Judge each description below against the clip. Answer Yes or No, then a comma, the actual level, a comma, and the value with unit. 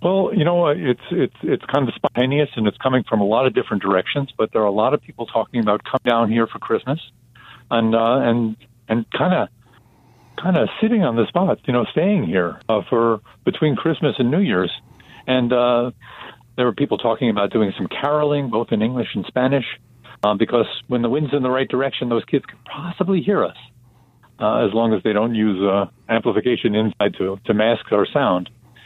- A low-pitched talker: Yes, low, 120 Hz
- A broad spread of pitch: No, average, 3.2 semitones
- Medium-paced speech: No, fast, 210 wpm